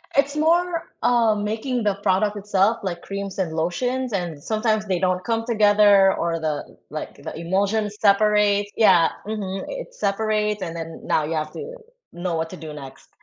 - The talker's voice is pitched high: Yes, high, 205 Hz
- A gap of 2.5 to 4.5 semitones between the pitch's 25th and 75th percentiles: Yes, average, 3.7 semitones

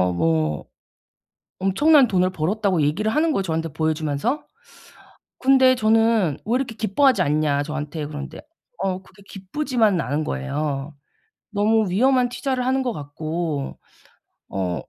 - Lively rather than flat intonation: Yes, wide, 7.6 semitones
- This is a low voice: No, medium, 185 Hz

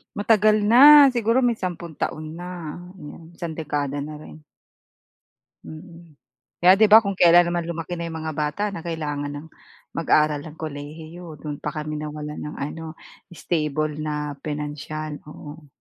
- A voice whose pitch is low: No, medium, 155 Hz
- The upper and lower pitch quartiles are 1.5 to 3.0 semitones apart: Yes, average, 2.7 semitones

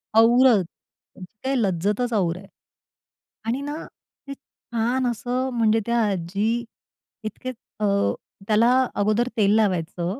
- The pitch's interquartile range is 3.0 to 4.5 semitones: Yes, average, 3.6 semitones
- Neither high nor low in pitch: No, high, 225 Hz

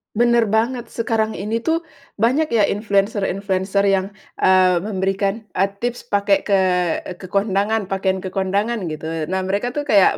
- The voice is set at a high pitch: Yes, high, 200 Hz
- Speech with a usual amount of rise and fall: Yes, average, 3.0 semitones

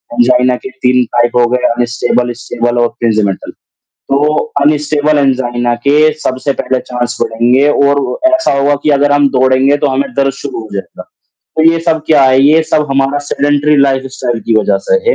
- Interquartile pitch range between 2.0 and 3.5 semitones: Yes, average, 2.9 semitones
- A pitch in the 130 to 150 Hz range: Yes, low, 135 Hz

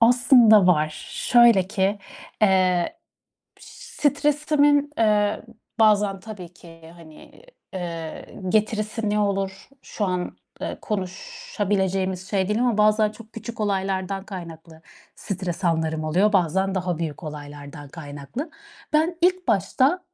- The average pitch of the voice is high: Yes, high, 195 Hz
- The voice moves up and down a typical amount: Yes, average, 3.9 semitones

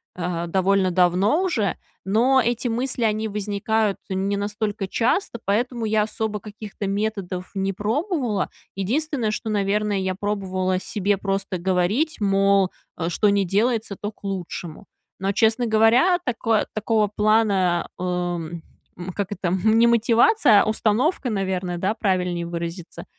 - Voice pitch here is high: Yes, high, 205 Hz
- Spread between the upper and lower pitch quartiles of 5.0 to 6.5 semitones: No, average, 2.9 semitones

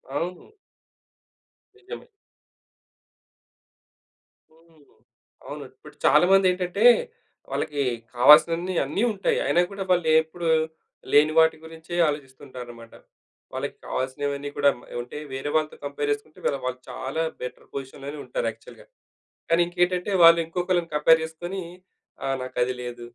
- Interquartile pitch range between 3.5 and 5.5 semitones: Yes, average, 3.9 semitones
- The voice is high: No, medium, 160 Hz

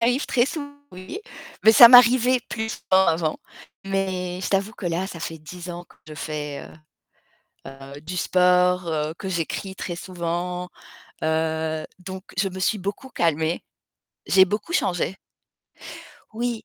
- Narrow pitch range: No, average, 3.5 semitones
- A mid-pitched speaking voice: Yes, medium, 180 Hz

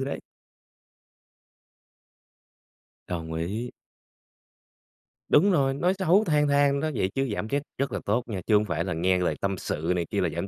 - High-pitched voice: No, low, 115 Hz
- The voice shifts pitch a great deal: Yes, wide, 7.8 semitones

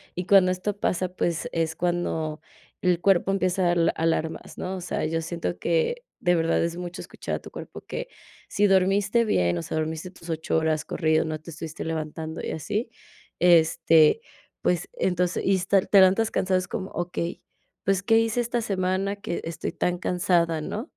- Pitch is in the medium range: Yes, medium, 175 Hz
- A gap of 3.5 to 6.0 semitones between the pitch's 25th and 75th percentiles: No, average, 2.8 semitones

